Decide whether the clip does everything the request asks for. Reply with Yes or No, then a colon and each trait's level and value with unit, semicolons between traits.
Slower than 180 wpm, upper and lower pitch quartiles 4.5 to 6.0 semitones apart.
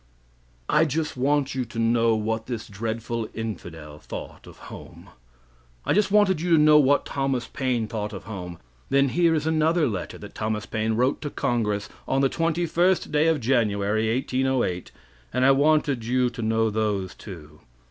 Yes: average, 170 wpm; average, 5.2 semitones